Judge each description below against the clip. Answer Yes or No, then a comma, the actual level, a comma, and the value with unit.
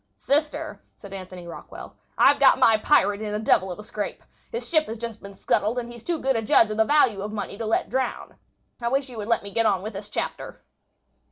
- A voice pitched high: Yes, high, 220 Hz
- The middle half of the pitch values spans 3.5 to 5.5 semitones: No, average, 3.0 semitones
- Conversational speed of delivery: No, fast, 240 wpm